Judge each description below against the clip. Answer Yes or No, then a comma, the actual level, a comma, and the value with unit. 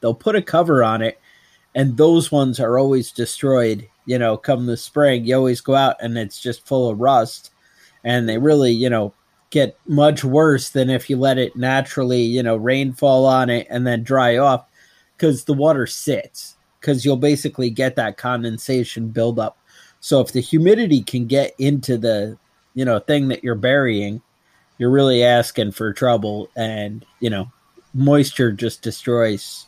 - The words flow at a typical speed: Yes, average, 175 wpm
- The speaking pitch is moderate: No, low, 125 Hz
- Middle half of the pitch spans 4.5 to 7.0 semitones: No, average, 2.9 semitones